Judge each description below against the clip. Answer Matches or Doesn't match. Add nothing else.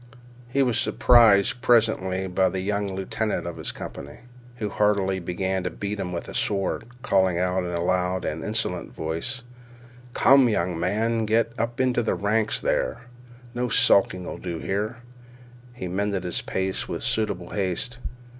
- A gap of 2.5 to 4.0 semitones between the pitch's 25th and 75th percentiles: Matches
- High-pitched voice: Doesn't match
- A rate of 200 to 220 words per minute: Doesn't match